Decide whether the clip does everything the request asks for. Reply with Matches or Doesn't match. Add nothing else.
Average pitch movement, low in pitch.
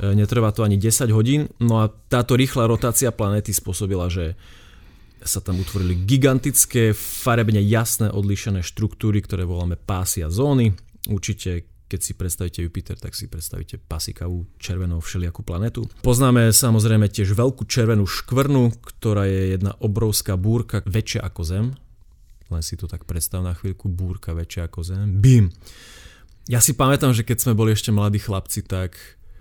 Matches